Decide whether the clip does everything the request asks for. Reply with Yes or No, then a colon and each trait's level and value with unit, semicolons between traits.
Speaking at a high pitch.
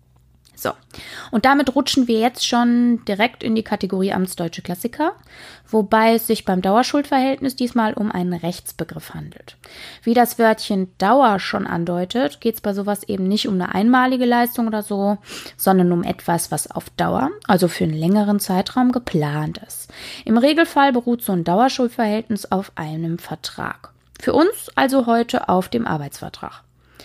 Yes: high, 215 Hz